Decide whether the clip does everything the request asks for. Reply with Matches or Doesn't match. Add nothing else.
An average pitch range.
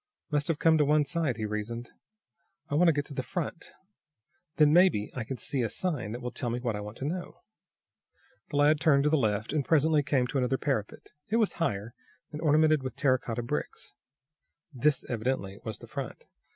Matches